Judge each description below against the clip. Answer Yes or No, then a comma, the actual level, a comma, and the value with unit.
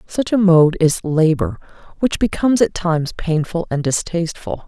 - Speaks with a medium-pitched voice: Yes, medium, 175 Hz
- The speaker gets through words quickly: No, average, 155 wpm